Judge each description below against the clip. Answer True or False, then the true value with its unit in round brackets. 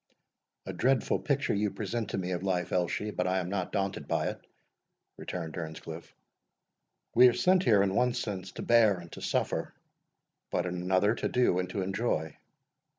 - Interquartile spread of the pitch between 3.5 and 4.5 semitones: True (4.2 semitones)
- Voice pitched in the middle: False (95 Hz)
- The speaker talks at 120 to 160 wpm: False (180 wpm)